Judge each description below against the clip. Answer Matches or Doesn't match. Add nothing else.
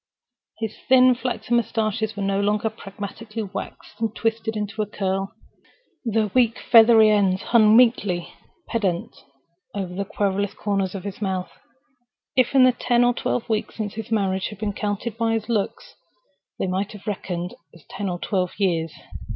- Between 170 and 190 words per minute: Doesn't match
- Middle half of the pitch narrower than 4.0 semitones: Matches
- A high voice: Matches